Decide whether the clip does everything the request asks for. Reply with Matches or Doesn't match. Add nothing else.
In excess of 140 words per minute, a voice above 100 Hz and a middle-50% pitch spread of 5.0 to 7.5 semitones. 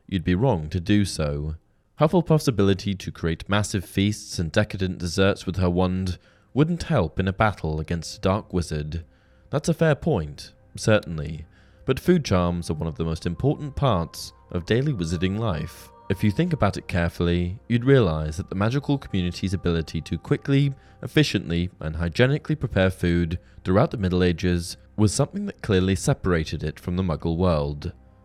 Doesn't match